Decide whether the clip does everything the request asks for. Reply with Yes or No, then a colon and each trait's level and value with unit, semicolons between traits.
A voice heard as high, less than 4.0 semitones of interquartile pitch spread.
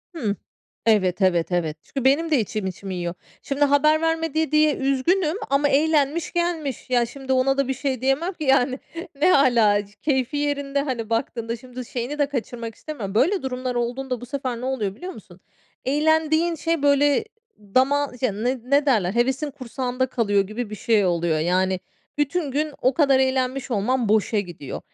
No: very high, 260 Hz; average, 4.3 semitones